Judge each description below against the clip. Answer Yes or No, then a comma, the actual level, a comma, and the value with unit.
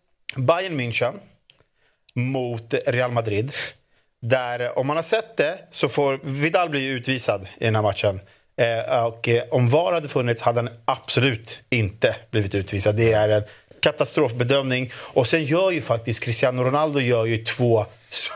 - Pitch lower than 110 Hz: No, low, 120 Hz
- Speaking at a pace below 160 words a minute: Yes, average, 150 wpm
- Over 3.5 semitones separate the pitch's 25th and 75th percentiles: No, average, 3.1 semitones